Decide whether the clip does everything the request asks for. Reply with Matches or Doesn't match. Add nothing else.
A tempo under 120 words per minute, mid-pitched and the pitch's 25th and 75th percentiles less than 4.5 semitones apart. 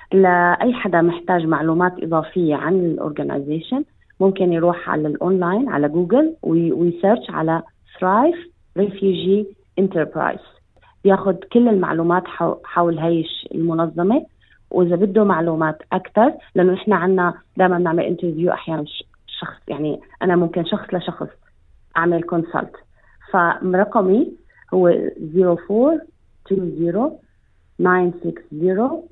Matches